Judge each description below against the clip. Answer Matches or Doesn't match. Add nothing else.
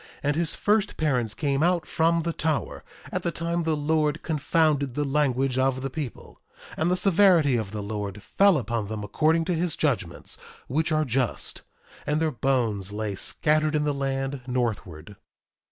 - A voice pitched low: Doesn't match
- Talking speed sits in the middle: Matches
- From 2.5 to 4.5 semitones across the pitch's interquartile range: Doesn't match